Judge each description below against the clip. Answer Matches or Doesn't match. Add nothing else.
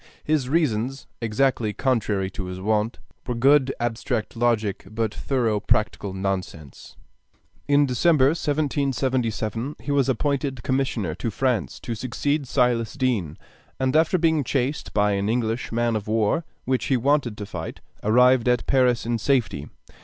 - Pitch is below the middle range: Matches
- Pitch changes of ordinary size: Matches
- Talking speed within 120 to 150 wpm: Matches